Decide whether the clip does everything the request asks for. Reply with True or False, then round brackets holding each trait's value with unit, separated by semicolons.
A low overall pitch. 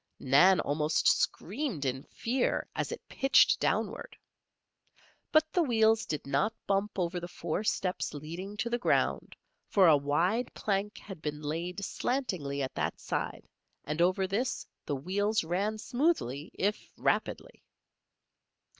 False (190 Hz)